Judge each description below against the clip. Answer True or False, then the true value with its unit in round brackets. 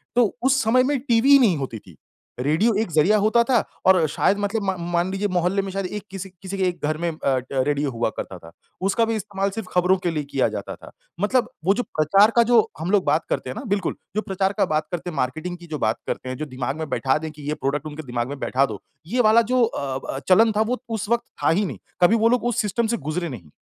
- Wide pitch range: True (6.5 semitones)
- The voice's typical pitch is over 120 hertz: True (185 Hz)